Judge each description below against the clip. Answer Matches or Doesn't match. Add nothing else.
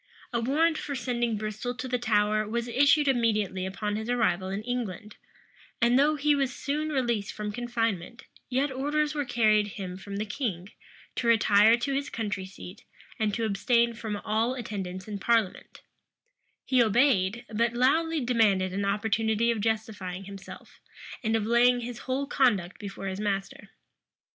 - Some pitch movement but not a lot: Matches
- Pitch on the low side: Doesn't match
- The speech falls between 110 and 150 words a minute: Doesn't match